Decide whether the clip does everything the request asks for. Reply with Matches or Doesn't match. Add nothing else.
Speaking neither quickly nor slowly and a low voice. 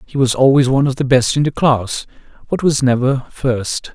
Doesn't match